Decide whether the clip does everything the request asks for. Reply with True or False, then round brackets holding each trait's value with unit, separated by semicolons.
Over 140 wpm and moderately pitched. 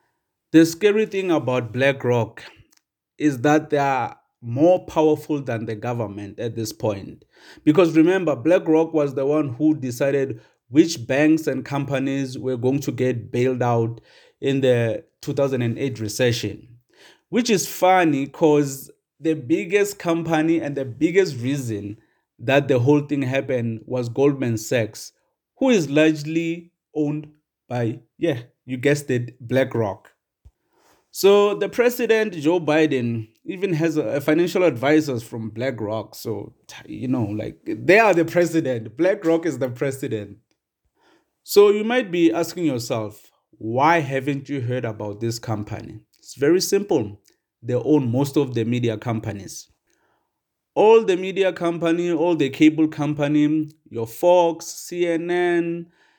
False (135 wpm; 145 Hz)